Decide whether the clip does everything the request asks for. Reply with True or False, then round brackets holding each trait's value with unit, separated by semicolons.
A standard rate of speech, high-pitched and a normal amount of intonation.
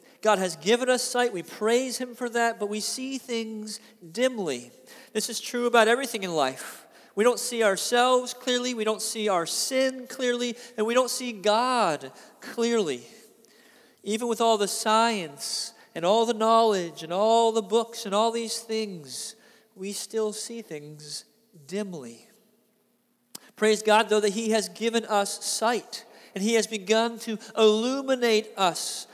False (160 wpm; 225 Hz; 1.9 semitones)